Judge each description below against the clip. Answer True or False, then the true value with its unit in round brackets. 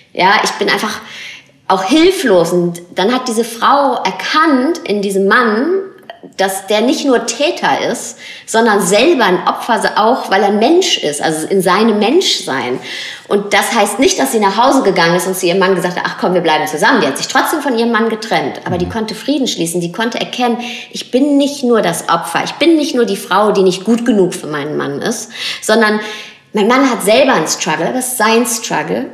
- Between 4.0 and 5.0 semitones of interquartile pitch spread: True (4.7 semitones)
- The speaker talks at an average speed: False (210 wpm)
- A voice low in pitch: False (215 Hz)